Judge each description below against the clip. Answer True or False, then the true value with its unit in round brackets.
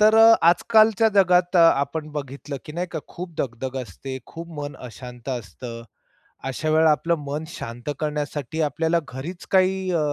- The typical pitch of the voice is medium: True (155 Hz)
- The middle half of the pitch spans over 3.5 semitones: True (5.0 semitones)